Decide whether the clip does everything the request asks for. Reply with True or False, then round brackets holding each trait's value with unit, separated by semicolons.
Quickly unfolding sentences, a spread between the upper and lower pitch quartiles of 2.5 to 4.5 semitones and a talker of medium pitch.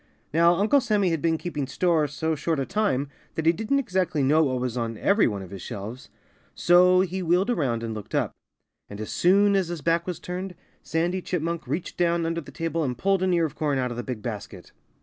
False (230 wpm; 5.6 semitones; 165 Hz)